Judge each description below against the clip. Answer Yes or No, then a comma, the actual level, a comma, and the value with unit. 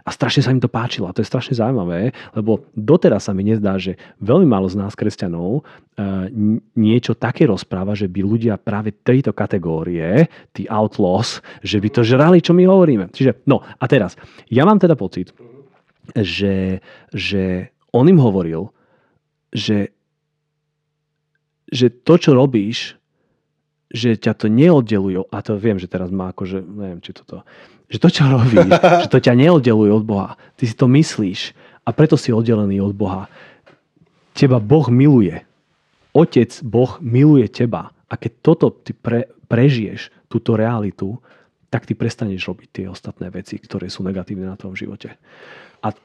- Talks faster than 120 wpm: Yes, average, 160 wpm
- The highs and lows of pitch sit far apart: Yes, wide, 5.7 semitones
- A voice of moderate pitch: No, low, 115 Hz